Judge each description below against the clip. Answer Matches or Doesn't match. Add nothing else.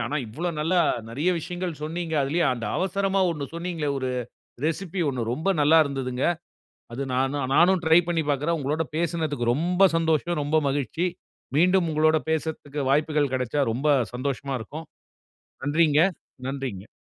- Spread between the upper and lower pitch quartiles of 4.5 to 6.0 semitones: Doesn't match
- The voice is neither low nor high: Matches